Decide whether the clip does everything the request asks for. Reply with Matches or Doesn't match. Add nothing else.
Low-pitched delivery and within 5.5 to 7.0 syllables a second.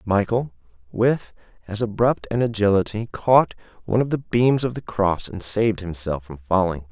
Doesn't match